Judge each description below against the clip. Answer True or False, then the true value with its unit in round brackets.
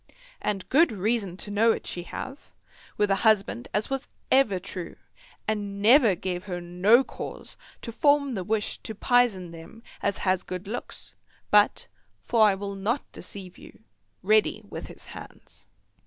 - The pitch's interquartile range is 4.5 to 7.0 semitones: False (3.4 semitones)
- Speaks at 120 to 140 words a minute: False (160 wpm)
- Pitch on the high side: True (205 Hz)